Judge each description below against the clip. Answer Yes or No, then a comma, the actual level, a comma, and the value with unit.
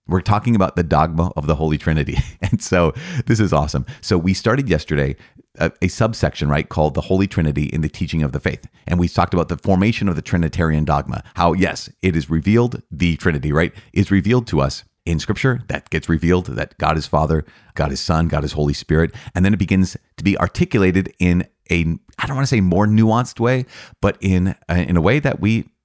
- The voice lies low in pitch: Yes, very low, 90 Hz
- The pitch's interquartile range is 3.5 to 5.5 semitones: Yes, average, 4.7 semitones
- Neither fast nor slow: No, fast, 220 wpm